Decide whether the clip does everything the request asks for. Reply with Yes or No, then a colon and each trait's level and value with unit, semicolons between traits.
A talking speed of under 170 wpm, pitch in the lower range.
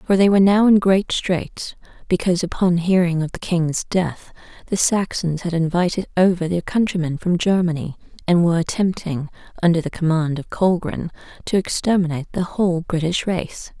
No: average, 160 wpm; medium, 175 Hz